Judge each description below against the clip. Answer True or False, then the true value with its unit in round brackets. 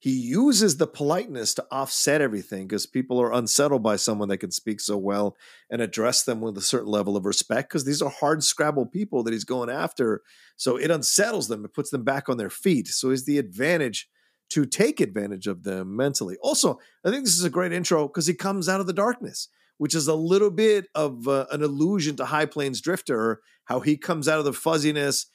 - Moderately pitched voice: True (145 Hz)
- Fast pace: True (220 wpm)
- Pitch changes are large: True (6.0 semitones)